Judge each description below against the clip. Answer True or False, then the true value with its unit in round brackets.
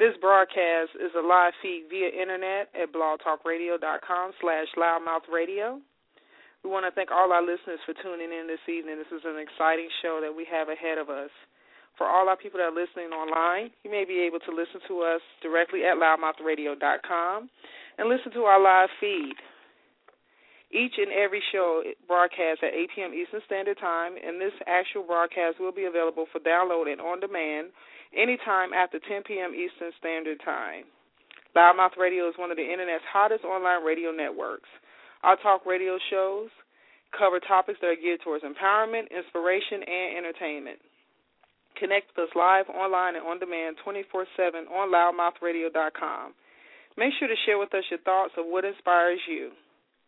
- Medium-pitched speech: True (180 Hz)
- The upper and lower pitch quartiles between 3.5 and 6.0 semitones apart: False (2.7 semitones)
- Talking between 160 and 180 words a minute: True (165 wpm)